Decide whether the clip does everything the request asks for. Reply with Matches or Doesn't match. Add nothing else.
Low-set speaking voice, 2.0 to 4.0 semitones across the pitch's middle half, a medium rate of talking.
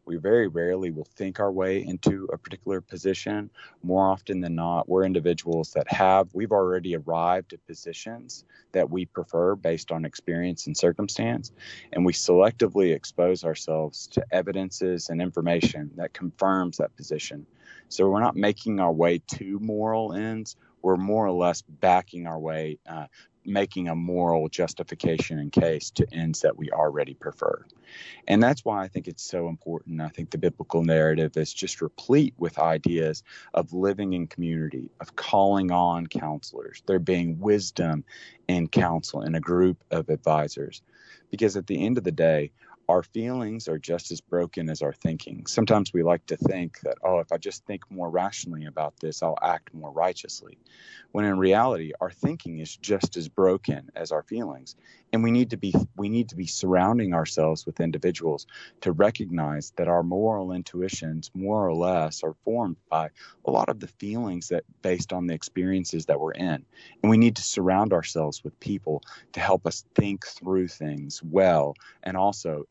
Matches